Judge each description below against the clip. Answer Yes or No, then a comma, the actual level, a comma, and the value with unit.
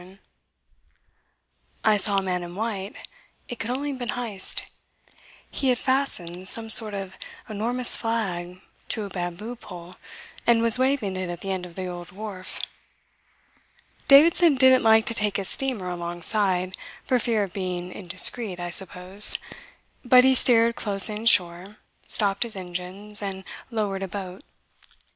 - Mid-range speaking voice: No, high, 205 Hz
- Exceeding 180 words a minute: No, average, 150 wpm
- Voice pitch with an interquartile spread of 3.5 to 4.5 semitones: Yes, average, 4.1 semitones